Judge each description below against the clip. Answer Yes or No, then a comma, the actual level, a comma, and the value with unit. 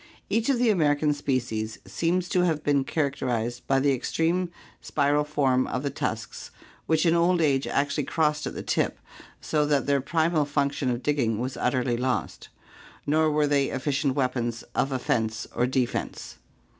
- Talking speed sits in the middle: Yes, average, 165 wpm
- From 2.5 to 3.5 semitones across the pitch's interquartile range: Yes, average, 3.2 semitones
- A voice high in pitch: No, medium, 140 Hz